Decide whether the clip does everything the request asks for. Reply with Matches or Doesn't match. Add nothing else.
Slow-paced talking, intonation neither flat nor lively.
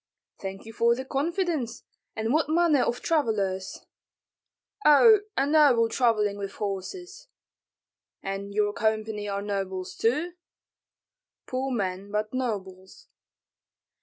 Doesn't match